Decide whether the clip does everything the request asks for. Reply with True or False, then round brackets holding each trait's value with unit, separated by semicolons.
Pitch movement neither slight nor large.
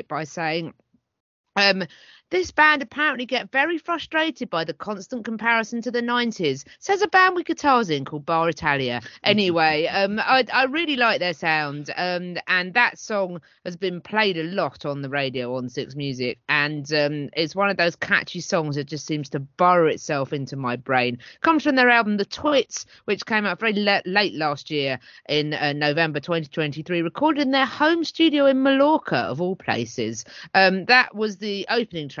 False (8.3 semitones)